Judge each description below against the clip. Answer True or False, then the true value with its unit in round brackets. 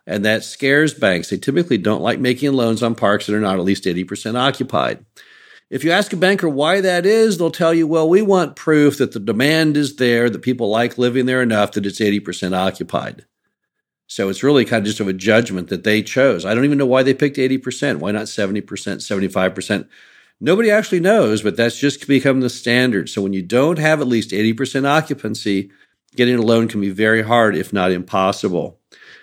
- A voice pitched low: True (120 Hz)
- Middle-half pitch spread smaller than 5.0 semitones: False (5.6 semitones)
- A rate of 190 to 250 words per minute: True (205 wpm)